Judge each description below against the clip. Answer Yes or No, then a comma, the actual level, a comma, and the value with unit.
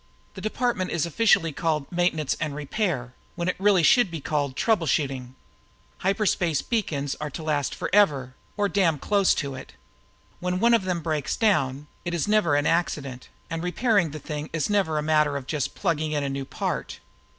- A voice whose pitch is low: No, medium, 160 Hz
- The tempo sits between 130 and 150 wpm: No, average, 185 wpm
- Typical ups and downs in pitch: Yes, average, 4.6 semitones